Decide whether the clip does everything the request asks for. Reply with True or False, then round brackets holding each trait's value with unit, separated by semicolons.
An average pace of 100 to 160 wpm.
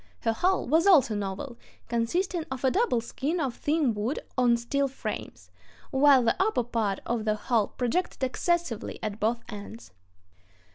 True (155 wpm)